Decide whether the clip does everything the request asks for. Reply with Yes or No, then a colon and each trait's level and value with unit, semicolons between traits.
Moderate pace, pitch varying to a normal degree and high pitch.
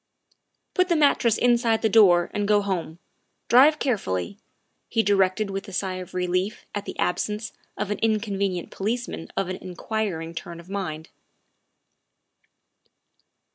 Yes: average, 155 wpm; average, 3.3 semitones; high, 200 Hz